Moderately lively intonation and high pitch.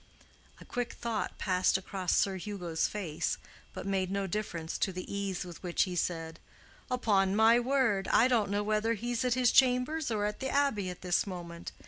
Yes: average, 4.3 semitones; high, 200 Hz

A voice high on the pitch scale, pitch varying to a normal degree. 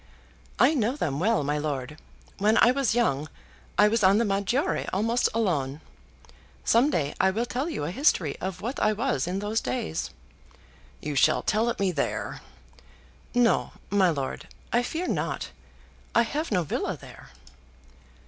No: high, 205 Hz; wide, 7.4 semitones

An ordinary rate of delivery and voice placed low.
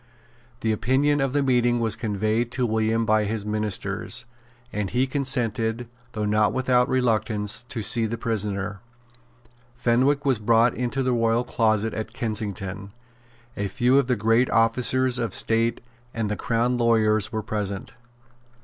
Yes: average, 150 wpm; low, 115 Hz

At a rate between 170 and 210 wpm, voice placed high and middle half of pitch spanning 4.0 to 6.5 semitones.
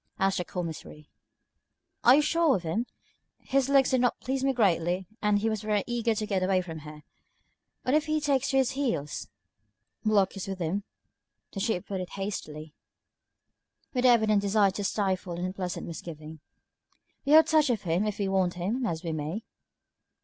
Yes: average, 185 wpm; high, 200 Hz; wide, 5.5 semitones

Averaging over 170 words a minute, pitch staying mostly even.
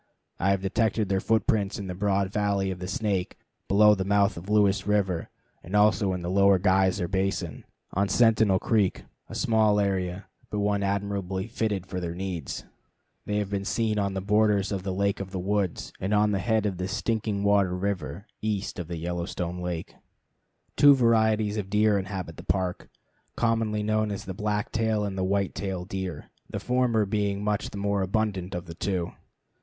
Yes: average, 180 wpm; narrow, 1.9 semitones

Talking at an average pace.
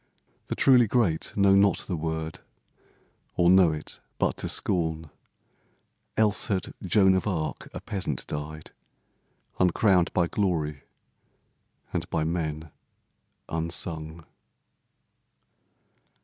No: slow, 105 wpm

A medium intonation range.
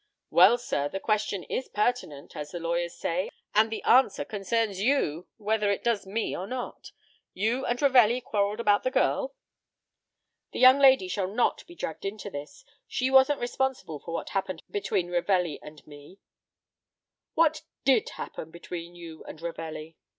No: wide, 6.1 semitones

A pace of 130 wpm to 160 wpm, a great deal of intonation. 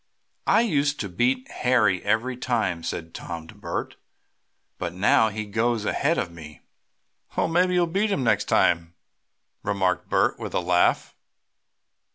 Yes: average, 150 wpm; wide, 6.9 semitones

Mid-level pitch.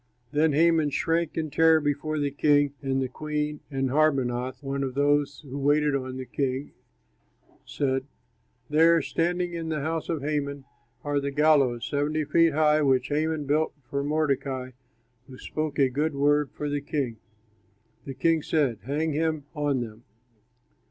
Yes: medium, 145 Hz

